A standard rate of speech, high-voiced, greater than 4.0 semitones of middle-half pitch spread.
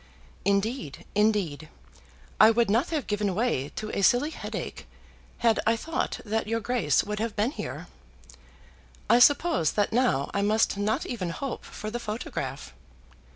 No: average, 155 wpm; high, 215 Hz; average, 3.2 semitones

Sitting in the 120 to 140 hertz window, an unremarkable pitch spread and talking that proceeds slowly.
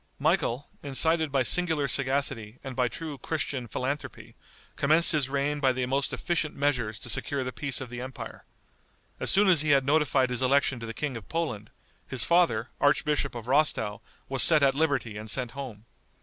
No: low, 135 Hz; average, 3.0 semitones; average, 185 wpm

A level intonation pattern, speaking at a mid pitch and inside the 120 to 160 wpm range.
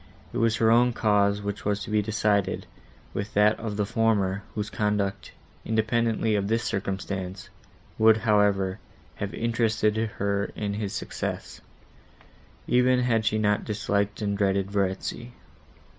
No: narrow, 1.7 semitones; low, 105 Hz; average, 140 wpm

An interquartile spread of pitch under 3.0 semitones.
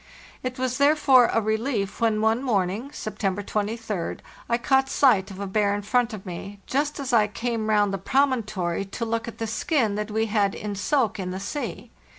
No: average, 3.6 semitones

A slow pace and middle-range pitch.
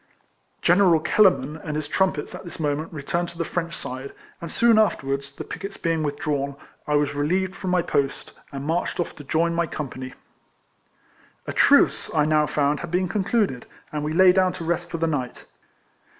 No: average, 190 wpm; medium, 160 Hz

